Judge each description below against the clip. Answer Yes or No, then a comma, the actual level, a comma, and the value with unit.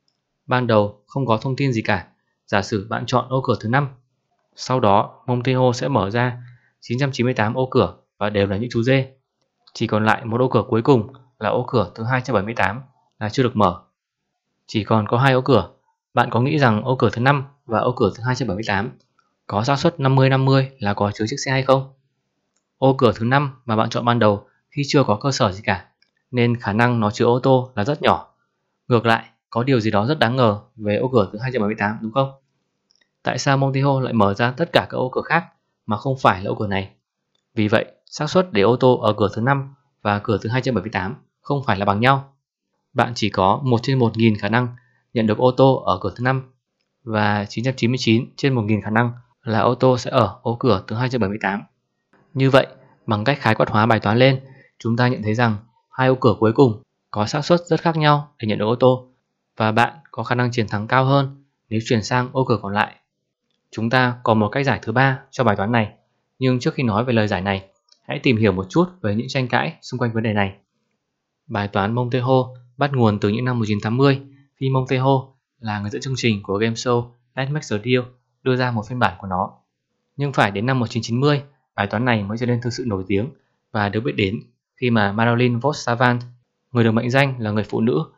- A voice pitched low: Yes, low, 120 Hz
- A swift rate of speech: No, average, 230 wpm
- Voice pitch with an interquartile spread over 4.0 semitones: No, average, 3.5 semitones